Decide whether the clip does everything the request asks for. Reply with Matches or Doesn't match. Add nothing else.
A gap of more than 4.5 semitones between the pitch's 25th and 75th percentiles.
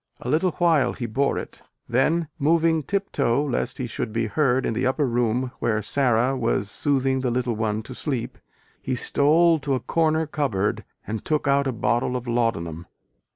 Doesn't match